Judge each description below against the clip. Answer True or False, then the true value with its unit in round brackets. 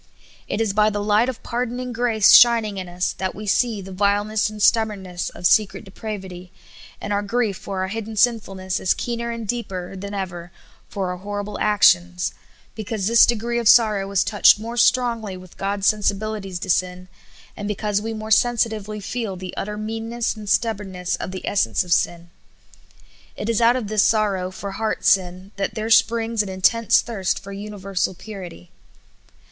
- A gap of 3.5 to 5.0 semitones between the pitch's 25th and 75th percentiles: False (2.9 semitones)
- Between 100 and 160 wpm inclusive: False (180 wpm)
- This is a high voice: True (205 Hz)